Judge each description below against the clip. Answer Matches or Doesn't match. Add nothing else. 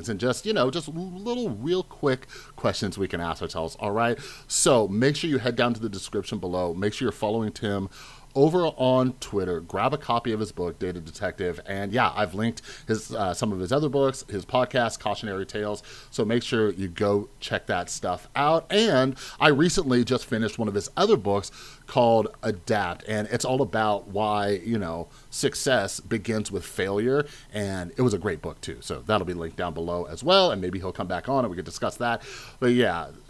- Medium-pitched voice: Doesn't match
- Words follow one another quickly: Matches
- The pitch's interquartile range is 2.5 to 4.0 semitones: Doesn't match